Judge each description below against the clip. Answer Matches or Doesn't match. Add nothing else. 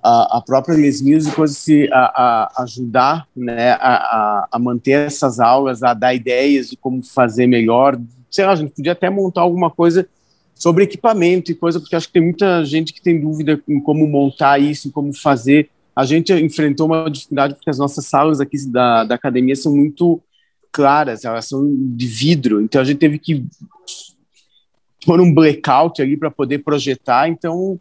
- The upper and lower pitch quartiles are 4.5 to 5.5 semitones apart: Doesn't match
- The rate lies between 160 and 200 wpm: Matches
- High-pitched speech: Doesn't match